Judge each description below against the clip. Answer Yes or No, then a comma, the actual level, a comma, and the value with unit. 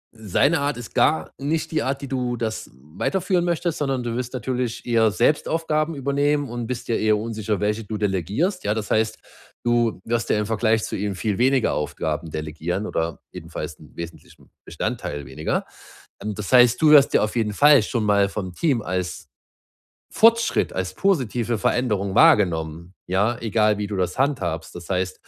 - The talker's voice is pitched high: No, low, 110 Hz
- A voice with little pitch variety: No, wide, 5.4 semitones